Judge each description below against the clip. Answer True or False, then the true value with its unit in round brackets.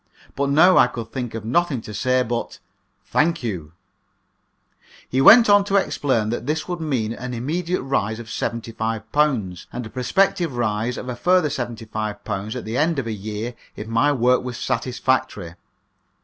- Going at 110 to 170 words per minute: True (165 wpm)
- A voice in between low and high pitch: False (125 Hz)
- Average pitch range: True (4.7 semitones)